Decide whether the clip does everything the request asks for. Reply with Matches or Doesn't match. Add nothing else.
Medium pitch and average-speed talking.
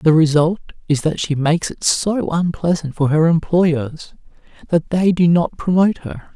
Matches